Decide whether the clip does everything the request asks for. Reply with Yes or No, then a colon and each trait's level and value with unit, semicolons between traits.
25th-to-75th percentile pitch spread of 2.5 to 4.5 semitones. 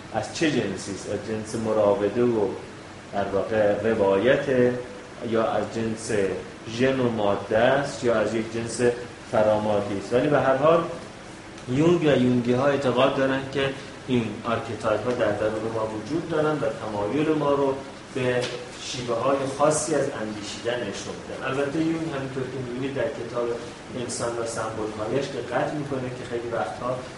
Yes: average, 3.8 semitones